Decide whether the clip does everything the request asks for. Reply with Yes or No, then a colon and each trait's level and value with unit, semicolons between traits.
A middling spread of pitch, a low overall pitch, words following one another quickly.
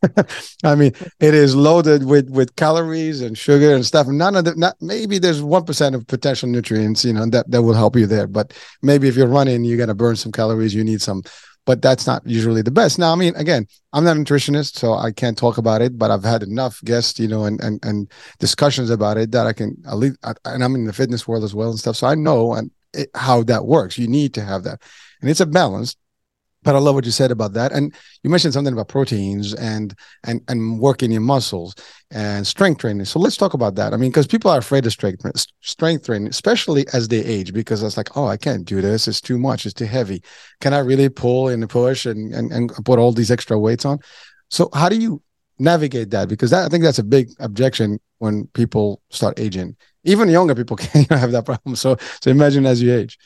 Yes: average, 4.5 semitones; low, 125 Hz; fast, 240 wpm